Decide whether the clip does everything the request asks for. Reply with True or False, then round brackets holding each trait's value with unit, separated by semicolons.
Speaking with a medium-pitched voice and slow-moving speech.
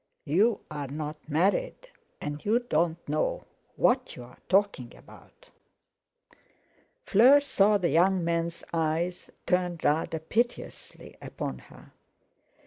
True (175 Hz; 105 wpm)